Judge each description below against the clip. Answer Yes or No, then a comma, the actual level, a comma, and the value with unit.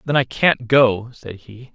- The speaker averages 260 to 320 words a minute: No, fast, 205 wpm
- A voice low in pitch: Yes, low, 120 Hz